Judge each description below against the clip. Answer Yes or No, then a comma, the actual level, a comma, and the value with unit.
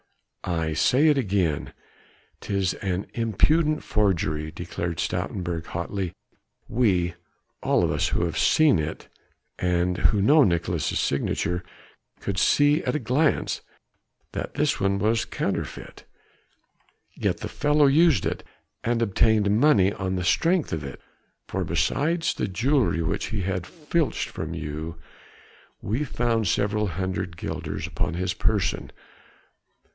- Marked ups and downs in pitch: Yes, wide, 6.7 semitones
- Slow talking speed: Yes, slow, 130 wpm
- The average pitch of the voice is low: Yes, low, 100 Hz